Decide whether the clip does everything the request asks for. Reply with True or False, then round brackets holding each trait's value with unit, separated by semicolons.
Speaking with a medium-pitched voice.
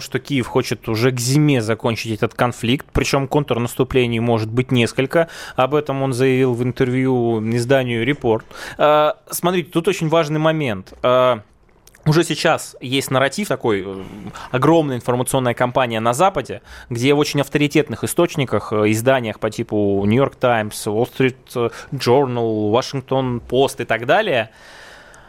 False (130 Hz)